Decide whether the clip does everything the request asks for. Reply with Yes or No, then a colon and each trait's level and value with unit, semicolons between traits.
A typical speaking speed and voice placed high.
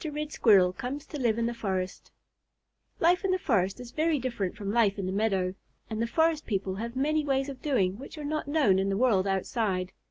No: fast, 220 wpm; high, 235 Hz